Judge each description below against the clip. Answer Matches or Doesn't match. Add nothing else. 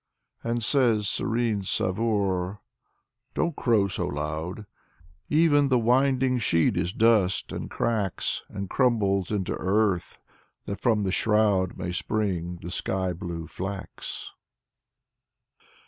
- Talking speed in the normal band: Doesn't match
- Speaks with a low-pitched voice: Matches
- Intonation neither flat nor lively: Matches